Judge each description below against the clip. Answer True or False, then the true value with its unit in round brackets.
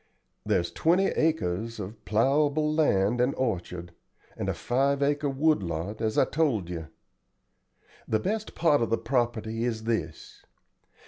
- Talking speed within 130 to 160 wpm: True (140 wpm)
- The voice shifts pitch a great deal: True (6.0 semitones)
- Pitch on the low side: True (115 Hz)